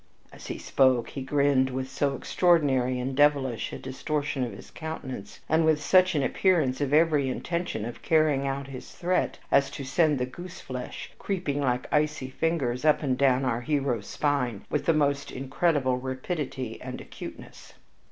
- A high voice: No, medium, 140 Hz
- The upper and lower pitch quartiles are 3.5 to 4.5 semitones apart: No, average, 3.0 semitones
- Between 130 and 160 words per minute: No, average, 170 wpm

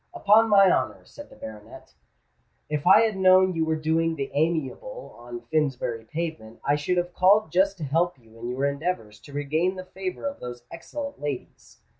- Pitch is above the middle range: No, medium, 160 Hz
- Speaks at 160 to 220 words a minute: Yes, average, 185 wpm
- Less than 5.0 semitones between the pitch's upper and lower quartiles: No, average, 5.3 semitones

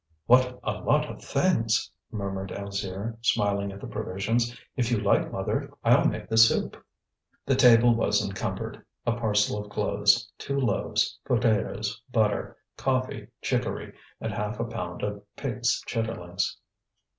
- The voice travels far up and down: No, average, 2.8 semitones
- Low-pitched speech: Yes, low, 110 Hz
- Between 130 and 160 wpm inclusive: Yes, average, 140 wpm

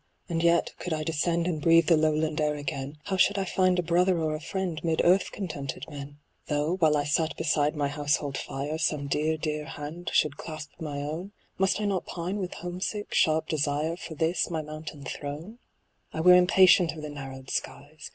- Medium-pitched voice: Yes, medium, 155 Hz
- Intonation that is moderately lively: Yes, average, 3.0 semitones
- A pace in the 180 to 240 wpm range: Yes, average, 200 wpm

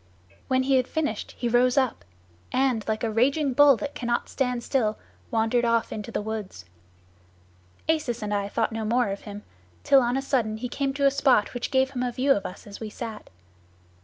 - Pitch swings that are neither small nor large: Yes, average, 3.4 semitones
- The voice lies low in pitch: No, high, 240 Hz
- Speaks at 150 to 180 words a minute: No, fast, 205 wpm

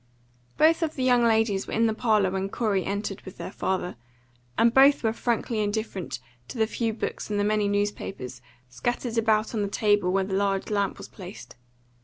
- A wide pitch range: No, average, 2.7 semitones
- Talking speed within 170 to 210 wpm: Yes, average, 195 wpm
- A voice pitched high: Yes, high, 210 Hz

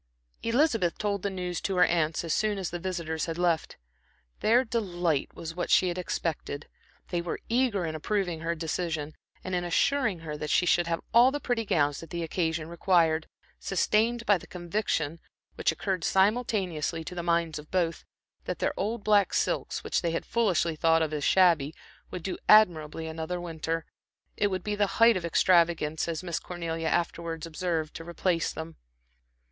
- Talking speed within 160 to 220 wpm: Yes, average, 180 wpm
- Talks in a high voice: No, medium, 175 Hz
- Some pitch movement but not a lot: Yes, average, 3.0 semitones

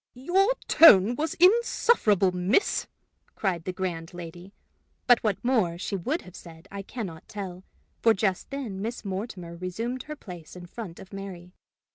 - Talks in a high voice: Yes, high, 195 Hz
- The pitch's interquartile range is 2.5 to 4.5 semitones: No, average, 5.2 semitones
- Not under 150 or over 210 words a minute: Yes, average, 160 wpm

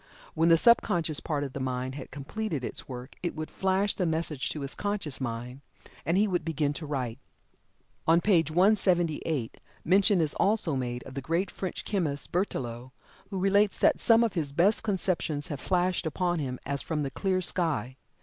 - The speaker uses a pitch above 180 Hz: No, medium, 160 Hz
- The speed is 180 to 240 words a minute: Yes, average, 185 wpm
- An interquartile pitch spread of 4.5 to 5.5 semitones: Yes, average, 5.2 semitones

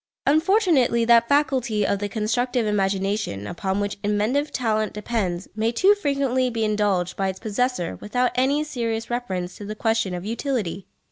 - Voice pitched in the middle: No, high, 225 Hz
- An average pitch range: Yes, average, 3.9 semitones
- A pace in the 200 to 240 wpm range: No, average, 155 wpm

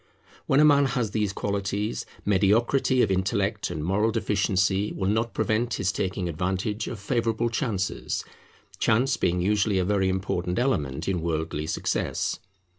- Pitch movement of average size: Yes, average, 3.3 semitones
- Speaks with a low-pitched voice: Yes, low, 100 Hz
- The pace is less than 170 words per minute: Yes, average, 145 wpm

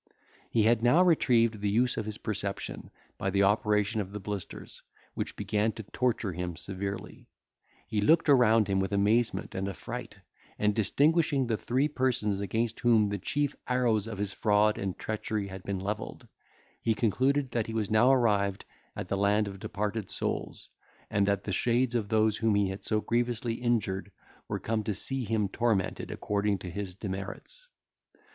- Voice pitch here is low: Yes, low, 105 Hz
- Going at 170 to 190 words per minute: Yes, average, 175 wpm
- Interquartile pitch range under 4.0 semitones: Yes, average, 2.8 semitones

